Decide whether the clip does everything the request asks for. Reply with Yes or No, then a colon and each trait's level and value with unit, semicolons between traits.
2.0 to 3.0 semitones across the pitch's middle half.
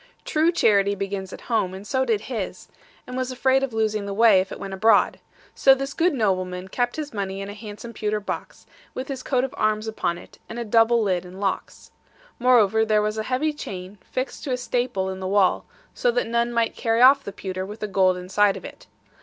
No: average, 4.1 semitones